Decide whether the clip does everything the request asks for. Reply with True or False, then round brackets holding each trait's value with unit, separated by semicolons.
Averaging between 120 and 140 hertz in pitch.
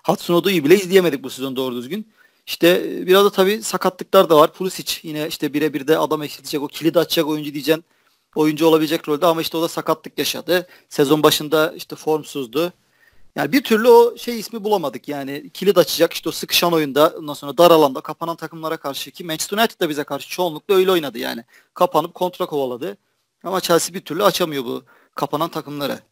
False (160 Hz)